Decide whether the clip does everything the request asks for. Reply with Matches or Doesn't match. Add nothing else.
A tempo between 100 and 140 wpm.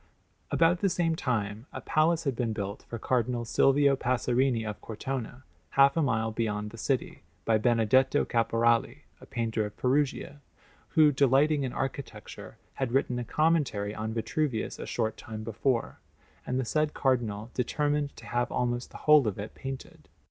Doesn't match